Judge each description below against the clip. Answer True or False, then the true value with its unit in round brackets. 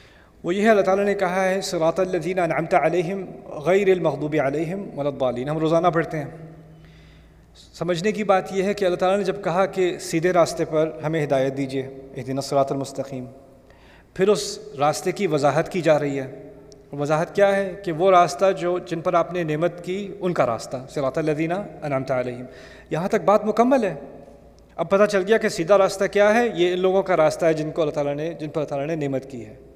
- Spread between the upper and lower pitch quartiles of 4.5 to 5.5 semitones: True (5.2 semitones)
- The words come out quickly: True (210 wpm)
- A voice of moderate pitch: True (165 Hz)